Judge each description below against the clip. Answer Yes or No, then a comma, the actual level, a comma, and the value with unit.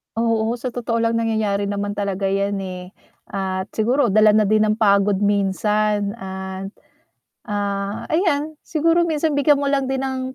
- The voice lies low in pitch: No, high, 215 Hz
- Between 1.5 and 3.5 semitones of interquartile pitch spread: No, average, 4.5 semitones